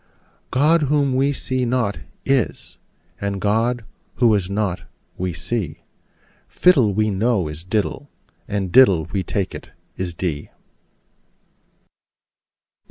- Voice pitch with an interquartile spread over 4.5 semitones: Yes, wide, 5.4 semitones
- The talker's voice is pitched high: No, low, 105 Hz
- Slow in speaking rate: Yes, slow, 115 wpm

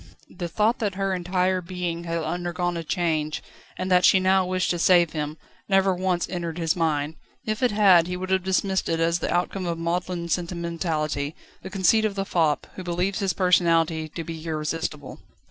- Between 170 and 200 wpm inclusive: Yes, average, 190 wpm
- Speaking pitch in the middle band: Yes, medium, 175 Hz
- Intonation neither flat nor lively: No, narrow, 2.2 semitones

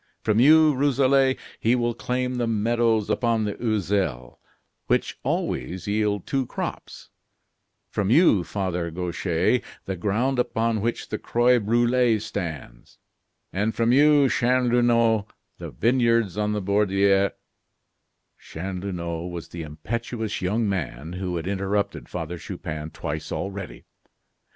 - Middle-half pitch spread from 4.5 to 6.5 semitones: Yes, average, 4.9 semitones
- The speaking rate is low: Yes, slow, 120 wpm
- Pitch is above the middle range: No, low, 105 Hz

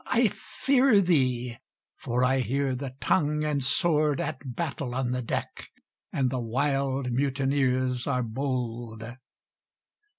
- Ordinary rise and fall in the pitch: No, narrow, 2.2 semitones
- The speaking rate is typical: No, slow, 125 wpm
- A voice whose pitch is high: No, low, 130 Hz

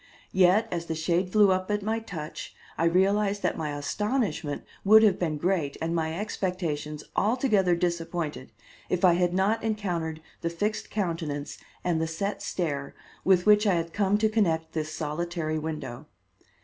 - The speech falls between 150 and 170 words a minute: Yes, average, 160 wpm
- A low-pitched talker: No, medium, 175 Hz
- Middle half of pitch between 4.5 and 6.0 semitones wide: No, average, 4.1 semitones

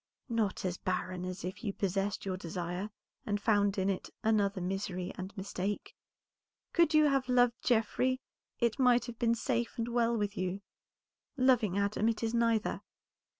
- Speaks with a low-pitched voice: No, high, 210 Hz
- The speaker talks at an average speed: Yes, average, 160 wpm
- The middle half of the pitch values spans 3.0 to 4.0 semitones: Yes, average, 3.7 semitones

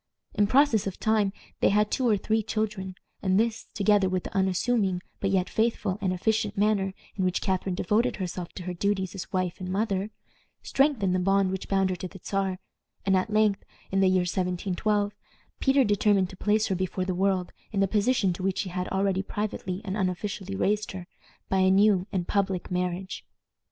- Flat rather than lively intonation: Yes, narrow, 2.1 semitones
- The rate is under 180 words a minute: No, average, 195 wpm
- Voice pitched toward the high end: Yes, high, 195 Hz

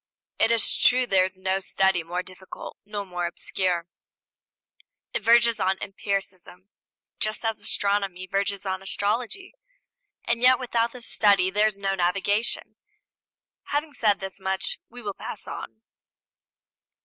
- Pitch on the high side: Yes, high, 200 Hz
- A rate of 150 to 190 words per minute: No, slow, 135 wpm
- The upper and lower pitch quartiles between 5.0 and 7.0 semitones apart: No, average, 3.0 semitones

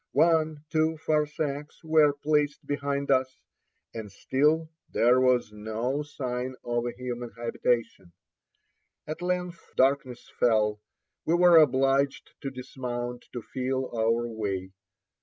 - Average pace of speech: No, slow, 120 wpm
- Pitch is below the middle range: Yes, low, 130 Hz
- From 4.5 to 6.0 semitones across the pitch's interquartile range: No, average, 3.7 semitones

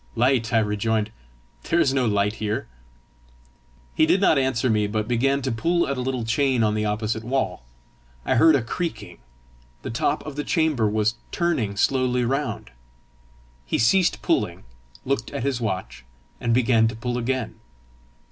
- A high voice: No, low, 120 Hz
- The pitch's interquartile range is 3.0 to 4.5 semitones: Yes, average, 3.8 semitones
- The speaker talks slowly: No, average, 165 wpm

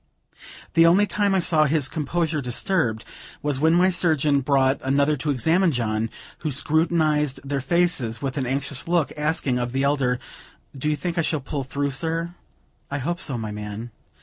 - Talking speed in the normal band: Yes, average, 175 wpm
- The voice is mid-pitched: Yes, medium, 145 Hz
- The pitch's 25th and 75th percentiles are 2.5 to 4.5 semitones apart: Yes, average, 3.9 semitones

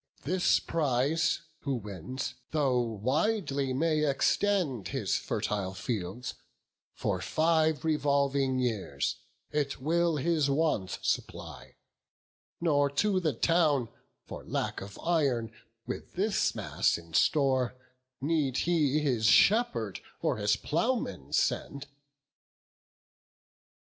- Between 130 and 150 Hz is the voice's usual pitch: Yes, medium, 140 Hz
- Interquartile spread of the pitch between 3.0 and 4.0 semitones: No, average, 5.0 semitones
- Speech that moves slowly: Yes, slow, 105 wpm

